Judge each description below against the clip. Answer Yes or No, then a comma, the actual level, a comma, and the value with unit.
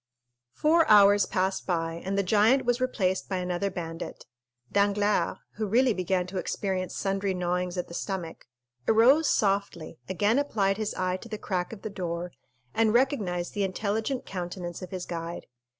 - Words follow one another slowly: No, average, 165 wpm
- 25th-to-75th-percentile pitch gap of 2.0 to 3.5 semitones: Yes, average, 3.0 semitones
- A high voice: Yes, high, 195 Hz